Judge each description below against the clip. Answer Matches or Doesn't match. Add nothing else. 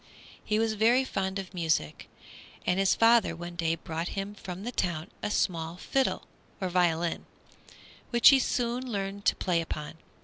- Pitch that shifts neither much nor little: Matches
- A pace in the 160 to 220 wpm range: Matches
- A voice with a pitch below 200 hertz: Matches